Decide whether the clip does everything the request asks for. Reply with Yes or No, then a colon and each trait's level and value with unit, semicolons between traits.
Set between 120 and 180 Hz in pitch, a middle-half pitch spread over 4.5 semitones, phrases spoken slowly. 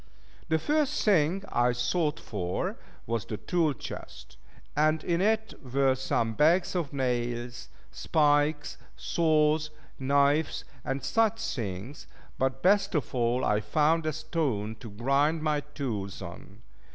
Yes: medium, 140 Hz; average, 4.9 semitones; slow, 130 wpm